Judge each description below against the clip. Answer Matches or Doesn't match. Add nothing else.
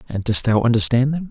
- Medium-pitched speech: Doesn't match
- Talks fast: Matches